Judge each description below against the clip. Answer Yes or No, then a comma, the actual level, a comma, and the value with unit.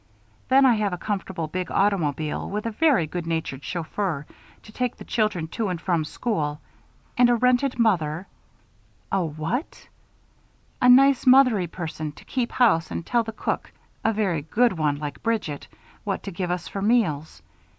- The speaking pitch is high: Yes, high, 195 Hz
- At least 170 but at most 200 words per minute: Yes, average, 175 wpm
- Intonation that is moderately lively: No, wide, 6.4 semitones